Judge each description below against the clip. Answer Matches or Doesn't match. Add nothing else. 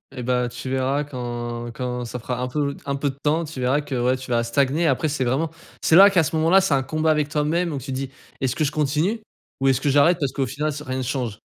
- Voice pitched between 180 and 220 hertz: Doesn't match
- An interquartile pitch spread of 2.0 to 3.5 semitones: Matches